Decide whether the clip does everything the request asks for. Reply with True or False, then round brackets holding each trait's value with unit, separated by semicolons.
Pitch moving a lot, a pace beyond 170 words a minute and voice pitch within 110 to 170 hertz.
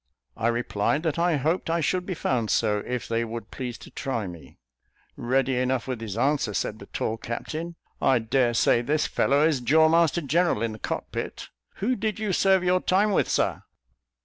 True (6.4 semitones; 190 wpm; 135 Hz)